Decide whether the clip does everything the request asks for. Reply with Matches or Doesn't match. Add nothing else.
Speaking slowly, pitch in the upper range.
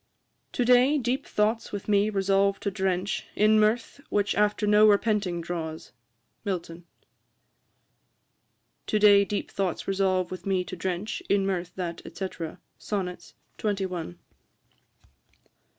Matches